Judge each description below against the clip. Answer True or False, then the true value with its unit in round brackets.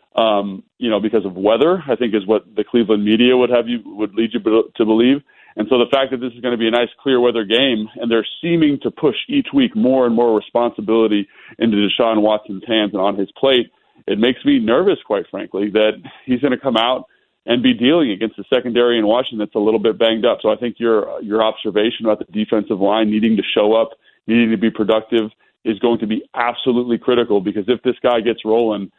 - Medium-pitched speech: False (115 Hz)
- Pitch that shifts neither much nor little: False (2.2 semitones)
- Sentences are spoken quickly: True (230 wpm)